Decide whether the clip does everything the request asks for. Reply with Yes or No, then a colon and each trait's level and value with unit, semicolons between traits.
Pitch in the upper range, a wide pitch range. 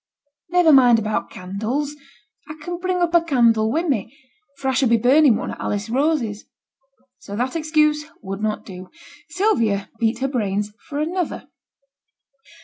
Yes: very high, 255 Hz; wide, 6.1 semitones